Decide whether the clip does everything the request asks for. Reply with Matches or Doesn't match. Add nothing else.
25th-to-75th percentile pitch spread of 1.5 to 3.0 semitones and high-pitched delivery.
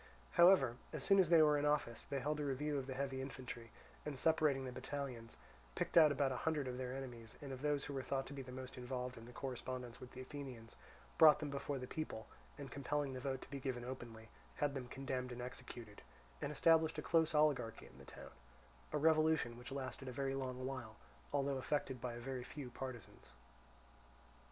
Doesn't match